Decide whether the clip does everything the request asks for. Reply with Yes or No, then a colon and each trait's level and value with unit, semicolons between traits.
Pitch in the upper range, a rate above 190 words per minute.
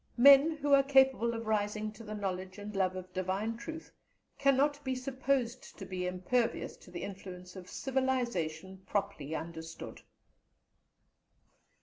No: high, 215 Hz; slow, 135 wpm